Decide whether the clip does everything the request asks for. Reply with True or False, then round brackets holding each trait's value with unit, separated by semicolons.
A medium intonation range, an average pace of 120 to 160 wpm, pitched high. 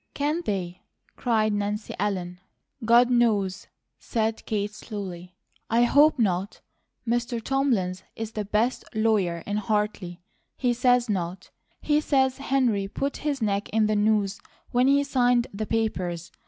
True (3.7 semitones; 140 wpm; 215 Hz)